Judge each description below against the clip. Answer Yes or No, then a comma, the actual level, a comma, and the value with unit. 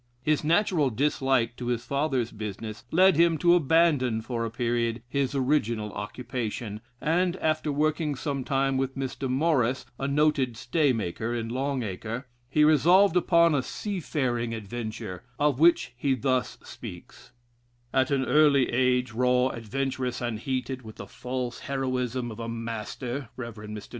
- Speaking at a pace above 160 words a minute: No, average, 150 wpm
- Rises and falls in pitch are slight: No, average, 3.8 semitones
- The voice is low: Yes, low, 130 Hz